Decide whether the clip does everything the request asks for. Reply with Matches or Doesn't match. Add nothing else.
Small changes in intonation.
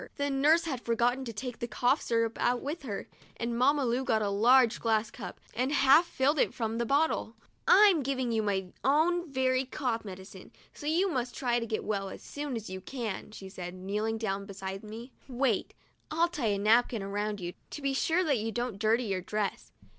Doesn't match